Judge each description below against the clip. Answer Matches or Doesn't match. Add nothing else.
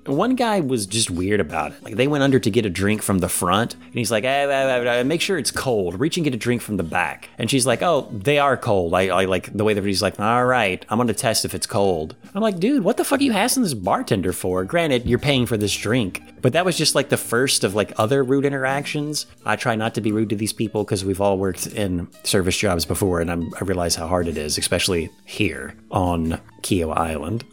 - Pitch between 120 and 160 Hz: Doesn't match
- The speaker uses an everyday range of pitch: Doesn't match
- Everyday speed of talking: Doesn't match